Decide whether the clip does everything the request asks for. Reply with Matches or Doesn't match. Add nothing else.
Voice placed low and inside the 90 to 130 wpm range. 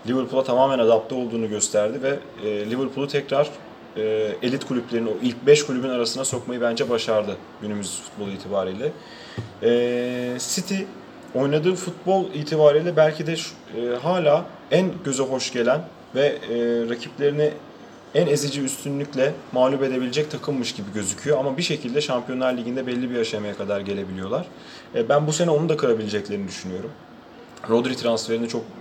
Doesn't match